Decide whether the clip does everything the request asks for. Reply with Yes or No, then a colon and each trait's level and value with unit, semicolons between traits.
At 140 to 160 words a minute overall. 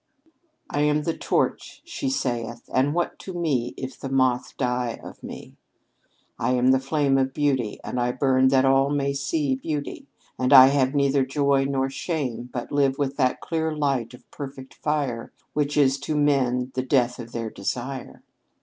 No: average, 175 wpm